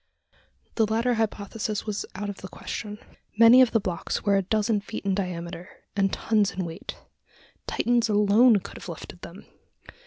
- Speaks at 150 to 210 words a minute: Yes, average, 165 wpm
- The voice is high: Yes, high, 205 Hz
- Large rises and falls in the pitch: No, narrow, 2.4 semitones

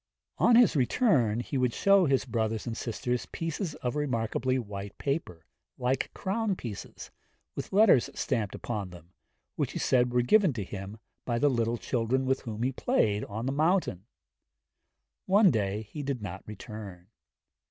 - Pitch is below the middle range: Yes, low, 125 Hz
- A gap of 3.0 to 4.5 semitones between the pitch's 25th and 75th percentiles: No, average, 5.2 semitones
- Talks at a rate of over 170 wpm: No, average, 160 wpm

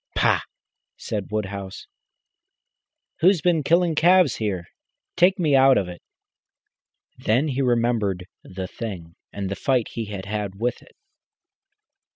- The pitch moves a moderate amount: No, wide, 6.6 semitones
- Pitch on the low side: Yes, low, 115 Hz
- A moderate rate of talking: No, slow, 130 wpm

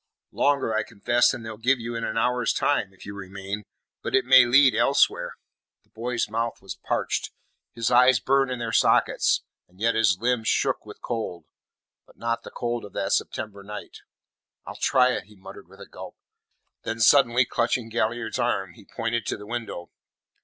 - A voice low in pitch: Yes, low, 115 Hz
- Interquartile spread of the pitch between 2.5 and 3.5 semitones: Yes, average, 3.0 semitones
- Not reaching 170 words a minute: No, average, 185 wpm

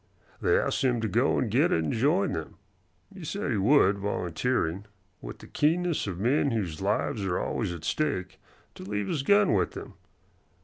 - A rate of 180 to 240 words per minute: Yes, average, 185 wpm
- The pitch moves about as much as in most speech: No, wide, 8.0 semitones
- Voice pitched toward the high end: No, low, 110 Hz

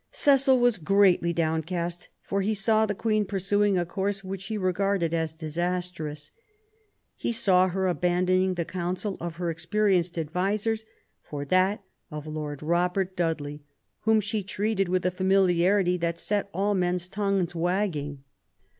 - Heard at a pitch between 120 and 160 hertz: No, medium, 185 Hz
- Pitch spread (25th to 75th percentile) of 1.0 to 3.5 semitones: Yes, average, 2.8 semitones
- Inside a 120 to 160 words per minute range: Yes, average, 145 wpm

